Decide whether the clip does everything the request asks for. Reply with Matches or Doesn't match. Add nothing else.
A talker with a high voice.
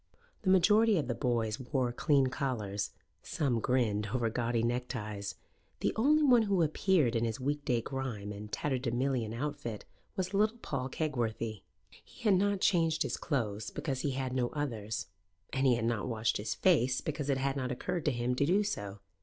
Doesn't match